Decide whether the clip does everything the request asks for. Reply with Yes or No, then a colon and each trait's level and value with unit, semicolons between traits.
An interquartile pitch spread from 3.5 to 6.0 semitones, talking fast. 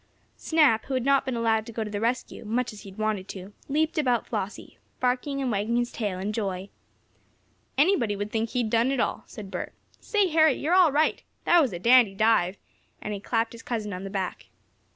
Yes: average, 4.1 semitones; fast, 215 wpm